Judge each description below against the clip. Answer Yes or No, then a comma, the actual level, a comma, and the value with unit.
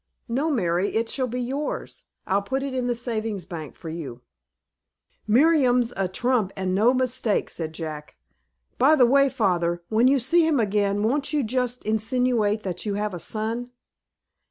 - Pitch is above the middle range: Yes, high, 225 Hz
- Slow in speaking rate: No, average, 170 wpm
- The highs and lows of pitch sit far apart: No, average, 4.7 semitones